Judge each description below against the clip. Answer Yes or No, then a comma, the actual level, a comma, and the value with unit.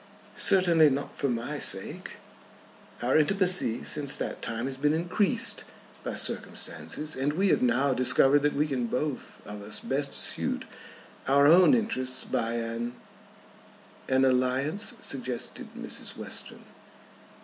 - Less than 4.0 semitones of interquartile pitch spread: Yes, average, 3.6 semitones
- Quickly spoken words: No, slow, 135 wpm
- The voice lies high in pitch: No, low, 135 Hz